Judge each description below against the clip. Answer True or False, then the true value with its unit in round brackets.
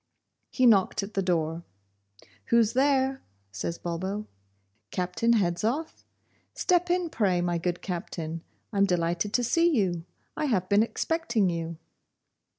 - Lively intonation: True (6.1 semitones)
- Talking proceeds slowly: True (130 wpm)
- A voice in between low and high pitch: False (195 Hz)